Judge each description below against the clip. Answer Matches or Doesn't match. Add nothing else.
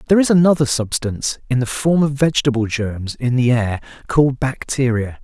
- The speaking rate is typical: Matches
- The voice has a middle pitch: Doesn't match